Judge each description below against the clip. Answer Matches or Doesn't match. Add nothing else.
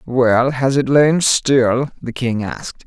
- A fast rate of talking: Doesn't match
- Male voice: Matches